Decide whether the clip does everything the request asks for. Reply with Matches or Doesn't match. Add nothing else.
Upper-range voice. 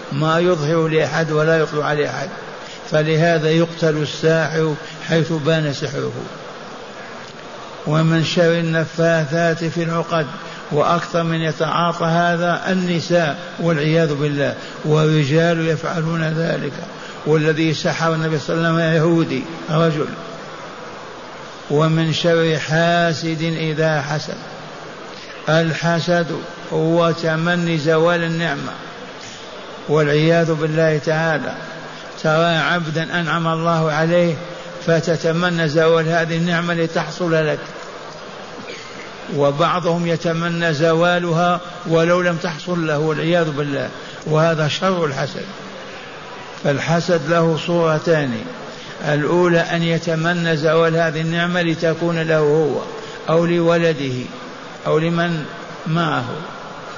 Doesn't match